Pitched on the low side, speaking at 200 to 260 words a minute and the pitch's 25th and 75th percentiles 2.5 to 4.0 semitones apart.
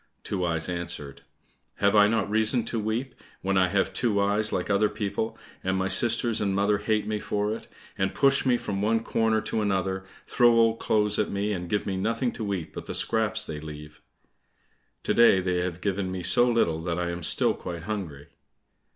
Yes: low, 100 Hz; fast, 205 wpm; average, 3.2 semitones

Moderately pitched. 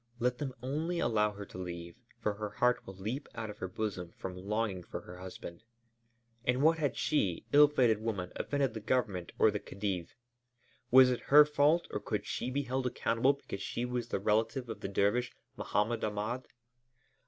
No: low, 115 Hz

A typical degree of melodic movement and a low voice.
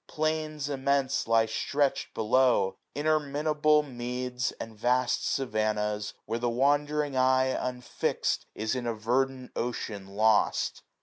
Yes: average, 4.0 semitones; low, 125 Hz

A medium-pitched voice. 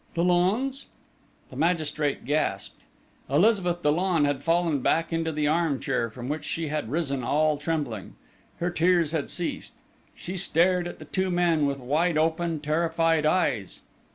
Yes: medium, 160 Hz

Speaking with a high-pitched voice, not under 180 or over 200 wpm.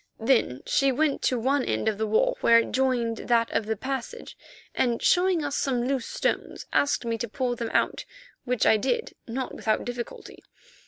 Yes: high, 245 Hz; average, 190 wpm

